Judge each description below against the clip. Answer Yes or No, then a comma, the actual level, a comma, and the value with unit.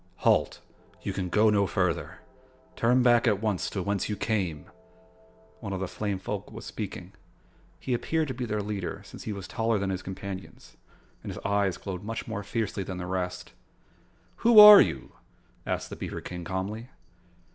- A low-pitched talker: Yes, low, 100 Hz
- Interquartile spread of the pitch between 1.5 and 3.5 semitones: Yes, average, 3.0 semitones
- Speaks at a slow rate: No, average, 180 wpm